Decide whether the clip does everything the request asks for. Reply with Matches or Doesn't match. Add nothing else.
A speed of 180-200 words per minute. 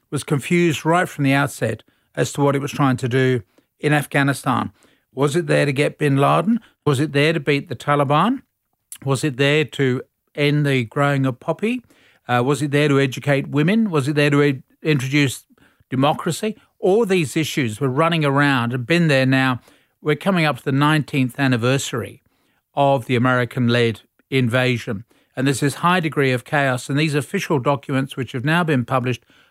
Matches